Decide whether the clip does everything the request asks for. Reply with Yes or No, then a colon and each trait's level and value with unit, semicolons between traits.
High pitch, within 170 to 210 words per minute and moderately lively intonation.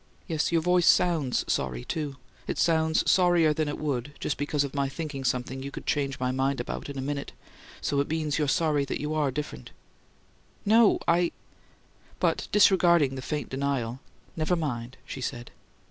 No: medium, 145 Hz; average, 175 wpm; average, 3.2 semitones